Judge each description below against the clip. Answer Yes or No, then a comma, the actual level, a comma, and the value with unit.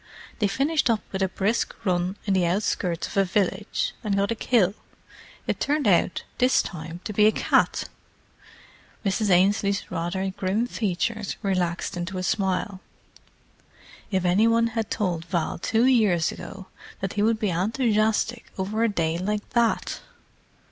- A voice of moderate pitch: No, high, 200 Hz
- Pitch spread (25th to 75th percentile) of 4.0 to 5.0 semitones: No, average, 3.3 semitones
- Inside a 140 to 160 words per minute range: Yes, average, 155 wpm